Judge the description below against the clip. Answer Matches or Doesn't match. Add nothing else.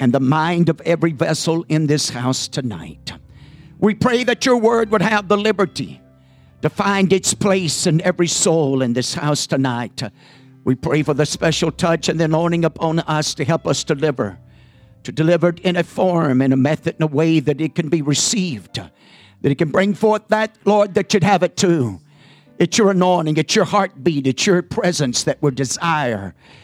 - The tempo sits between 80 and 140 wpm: Doesn't match